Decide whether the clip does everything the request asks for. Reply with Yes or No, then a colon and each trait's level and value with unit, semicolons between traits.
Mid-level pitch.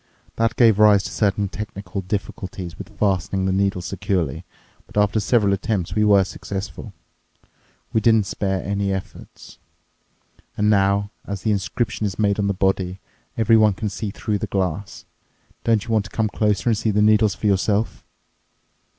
No: low, 100 Hz